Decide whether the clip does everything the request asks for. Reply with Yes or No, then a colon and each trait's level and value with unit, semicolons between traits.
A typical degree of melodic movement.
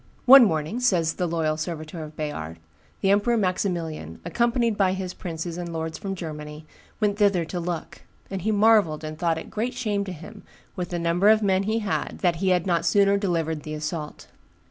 Yes: average, 4.0 semitones